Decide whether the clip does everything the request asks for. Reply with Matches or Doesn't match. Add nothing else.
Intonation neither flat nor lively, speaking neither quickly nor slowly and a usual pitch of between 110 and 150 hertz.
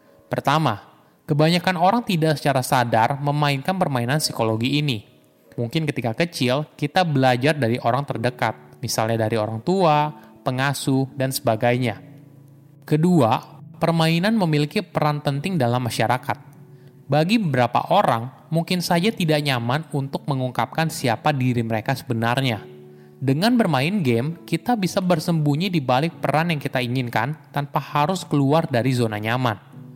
Matches